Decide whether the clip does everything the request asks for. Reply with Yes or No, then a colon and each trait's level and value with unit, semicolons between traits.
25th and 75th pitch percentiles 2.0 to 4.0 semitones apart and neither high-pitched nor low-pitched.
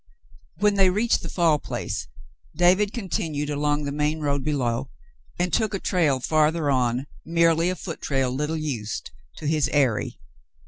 Yes: average, 3.6 semitones; medium, 150 Hz